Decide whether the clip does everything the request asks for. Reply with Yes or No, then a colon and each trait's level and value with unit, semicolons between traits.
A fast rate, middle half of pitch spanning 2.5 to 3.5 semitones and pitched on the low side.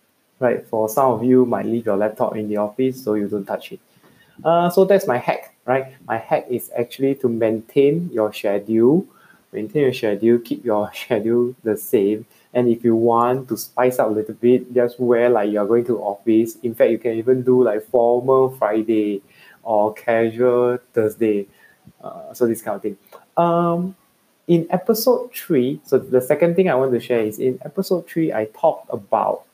No: average, 190 wpm; average, 3.1 semitones; low, 120 Hz